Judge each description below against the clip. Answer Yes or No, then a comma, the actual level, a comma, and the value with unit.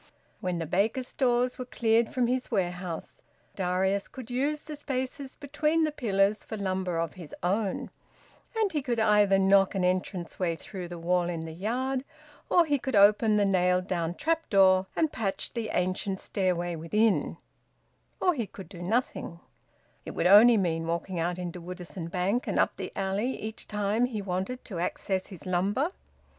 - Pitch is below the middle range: No, high, 195 Hz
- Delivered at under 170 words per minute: No, average, 175 wpm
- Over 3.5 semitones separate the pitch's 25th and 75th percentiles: Yes, average, 5.2 semitones